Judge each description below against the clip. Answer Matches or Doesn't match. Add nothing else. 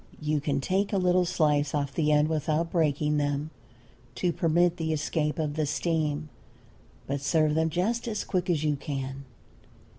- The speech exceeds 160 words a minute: Matches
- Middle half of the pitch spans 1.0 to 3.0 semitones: Matches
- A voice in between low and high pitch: Matches